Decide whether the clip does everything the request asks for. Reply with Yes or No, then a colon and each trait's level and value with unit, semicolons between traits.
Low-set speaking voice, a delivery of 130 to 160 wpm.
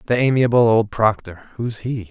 Yes: low, 110 Hz; average, 140 wpm